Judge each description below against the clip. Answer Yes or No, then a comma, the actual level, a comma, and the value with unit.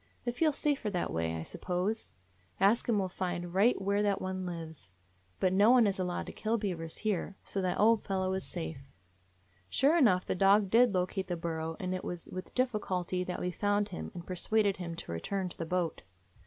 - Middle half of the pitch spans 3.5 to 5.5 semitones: No, average, 2.8 semitones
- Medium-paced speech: No, fast, 210 wpm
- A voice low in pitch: No, medium, 185 Hz